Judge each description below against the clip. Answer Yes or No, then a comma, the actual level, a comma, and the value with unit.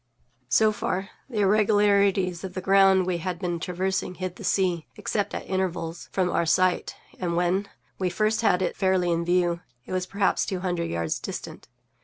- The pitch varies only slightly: Yes, narrow, 1.8 semitones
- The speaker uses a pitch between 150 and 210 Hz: Yes, medium, 185 Hz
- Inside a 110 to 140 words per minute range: No, average, 180 wpm